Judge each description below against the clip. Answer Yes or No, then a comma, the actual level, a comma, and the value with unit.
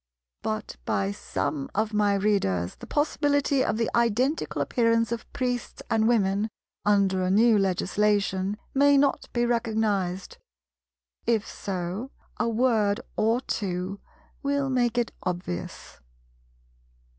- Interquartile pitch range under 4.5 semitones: Yes, average, 3.5 semitones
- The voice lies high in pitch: Yes, high, 220 Hz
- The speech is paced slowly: Yes, slow, 120 wpm